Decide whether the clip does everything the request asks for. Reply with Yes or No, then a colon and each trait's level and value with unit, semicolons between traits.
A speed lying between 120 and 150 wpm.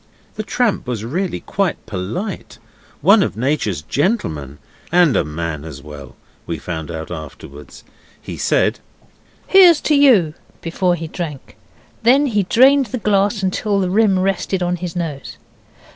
Yes: average, 145 wpm